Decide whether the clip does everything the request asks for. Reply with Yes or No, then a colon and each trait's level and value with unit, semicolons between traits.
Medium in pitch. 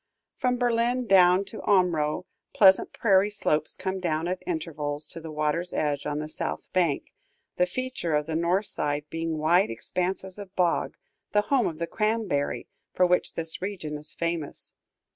Yes: medium, 175 Hz